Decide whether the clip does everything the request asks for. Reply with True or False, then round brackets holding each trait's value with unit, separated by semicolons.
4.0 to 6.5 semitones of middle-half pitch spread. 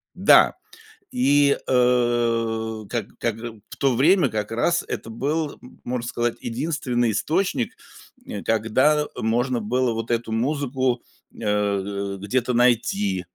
False (2.7 semitones)